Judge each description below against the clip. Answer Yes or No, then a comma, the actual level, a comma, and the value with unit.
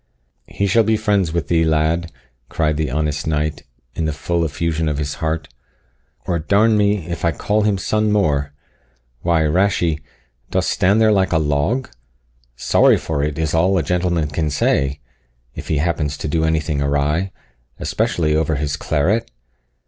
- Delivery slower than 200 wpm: Yes, average, 170 wpm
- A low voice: Yes, very low, 80 Hz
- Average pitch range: Yes, average, 3.6 semitones